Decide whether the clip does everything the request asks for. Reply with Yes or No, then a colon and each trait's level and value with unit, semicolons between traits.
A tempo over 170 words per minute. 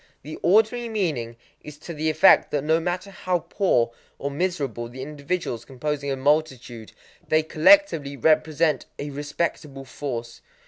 No: average, 140 wpm